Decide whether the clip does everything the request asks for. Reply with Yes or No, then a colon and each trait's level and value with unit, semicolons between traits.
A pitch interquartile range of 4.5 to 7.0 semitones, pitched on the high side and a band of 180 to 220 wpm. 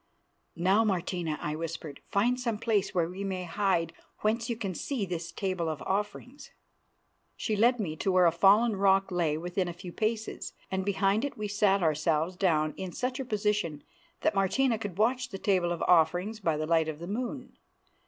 No: average, 4.1 semitones; high, 195 Hz; average, 190 wpm